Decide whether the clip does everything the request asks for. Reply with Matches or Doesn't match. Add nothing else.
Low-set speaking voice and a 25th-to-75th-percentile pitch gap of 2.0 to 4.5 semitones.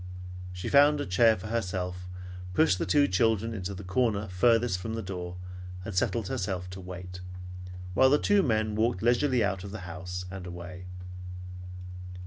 Matches